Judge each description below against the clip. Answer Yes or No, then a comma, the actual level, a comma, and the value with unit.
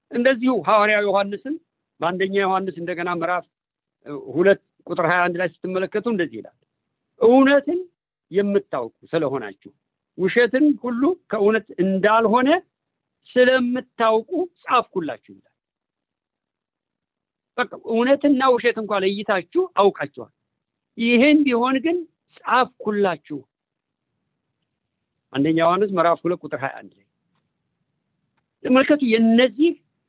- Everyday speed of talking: No, slow, 90 wpm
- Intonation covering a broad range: Yes, wide, 5.8 semitones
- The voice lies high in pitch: Yes, high, 220 Hz